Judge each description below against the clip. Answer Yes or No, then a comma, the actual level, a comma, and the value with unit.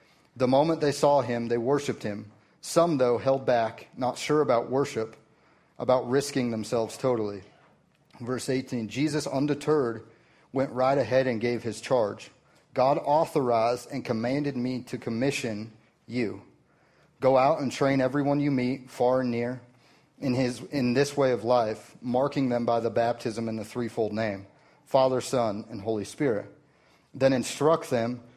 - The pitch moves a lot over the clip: No, average, 2.7 semitones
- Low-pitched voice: Yes, low, 125 Hz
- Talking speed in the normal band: Yes, average, 155 wpm